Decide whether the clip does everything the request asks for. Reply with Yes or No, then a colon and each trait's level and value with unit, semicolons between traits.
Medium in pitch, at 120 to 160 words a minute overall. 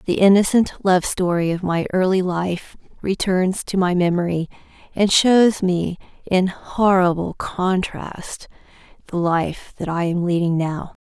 Yes: medium, 180 Hz; slow, 135 wpm